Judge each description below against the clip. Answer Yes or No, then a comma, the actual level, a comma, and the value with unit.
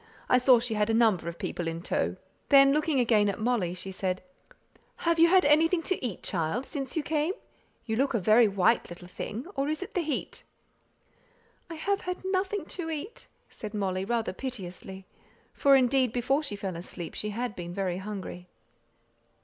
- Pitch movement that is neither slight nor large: No, wide, 7.5 semitones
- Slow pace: No, average, 185 wpm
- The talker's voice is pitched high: Yes, high, 240 Hz